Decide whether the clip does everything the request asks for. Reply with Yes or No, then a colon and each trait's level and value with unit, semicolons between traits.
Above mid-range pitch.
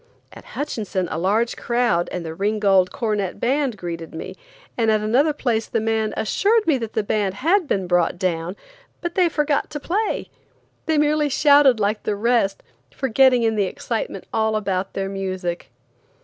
Yes: high, 220 Hz